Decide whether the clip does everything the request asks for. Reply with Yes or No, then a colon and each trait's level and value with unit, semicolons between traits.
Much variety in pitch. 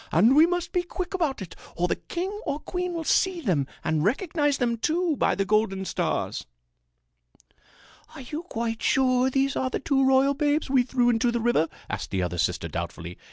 Yes: wide, 7.7 semitones